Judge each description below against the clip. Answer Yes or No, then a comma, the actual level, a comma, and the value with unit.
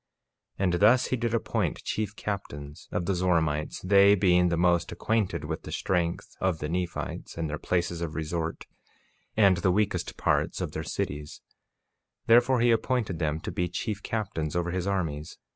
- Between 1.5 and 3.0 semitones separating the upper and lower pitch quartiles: No, average, 3.8 semitones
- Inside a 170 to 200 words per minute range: Yes, average, 175 wpm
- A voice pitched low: Yes, very low, 90 Hz